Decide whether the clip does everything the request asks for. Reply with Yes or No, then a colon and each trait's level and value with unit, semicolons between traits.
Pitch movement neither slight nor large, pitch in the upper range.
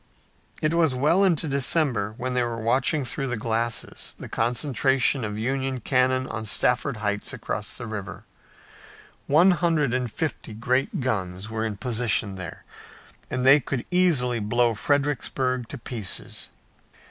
No: average, 3.7 semitones; low, 125 Hz